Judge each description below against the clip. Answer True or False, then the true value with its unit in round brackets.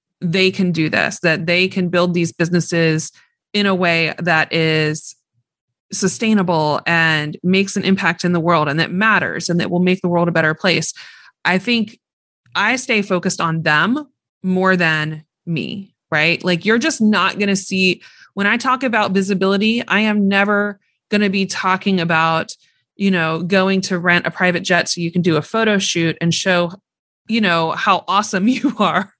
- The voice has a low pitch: False (185 Hz)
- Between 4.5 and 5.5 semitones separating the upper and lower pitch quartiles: False (3.4 semitones)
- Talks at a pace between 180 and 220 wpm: True (185 wpm)